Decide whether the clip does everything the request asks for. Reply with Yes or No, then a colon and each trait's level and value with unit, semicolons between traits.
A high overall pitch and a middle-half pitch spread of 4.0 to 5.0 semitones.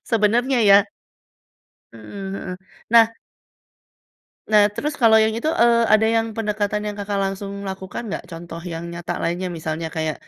Yes: high, 205 Hz; average, 4.4 semitones